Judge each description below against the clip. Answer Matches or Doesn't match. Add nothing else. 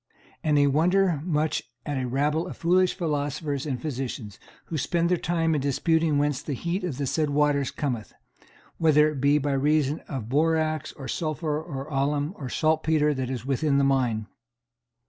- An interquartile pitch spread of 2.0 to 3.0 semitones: Matches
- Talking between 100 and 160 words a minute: Doesn't match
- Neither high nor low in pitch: Matches